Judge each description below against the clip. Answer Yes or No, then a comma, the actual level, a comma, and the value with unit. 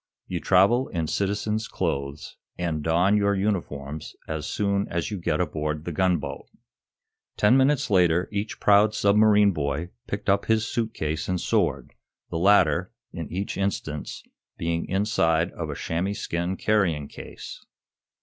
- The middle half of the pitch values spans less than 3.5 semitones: No, average, 4.3 semitones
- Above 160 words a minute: No, average, 145 wpm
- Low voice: Yes, very low, 90 Hz